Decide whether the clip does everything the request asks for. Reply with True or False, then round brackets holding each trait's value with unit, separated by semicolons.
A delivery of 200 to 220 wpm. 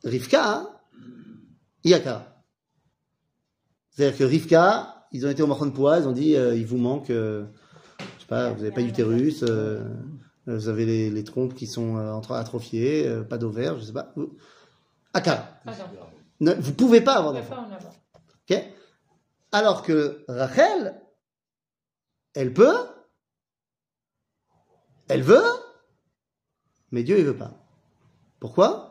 False (145 wpm)